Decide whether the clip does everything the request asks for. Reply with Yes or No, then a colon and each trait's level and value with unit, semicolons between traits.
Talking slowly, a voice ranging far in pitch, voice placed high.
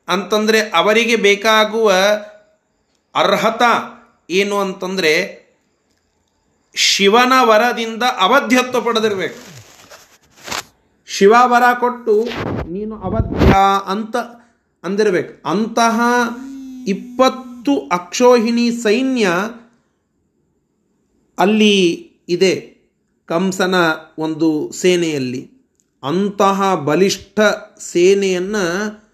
No: slow, 60 wpm; average, 3.9 semitones; high, 210 Hz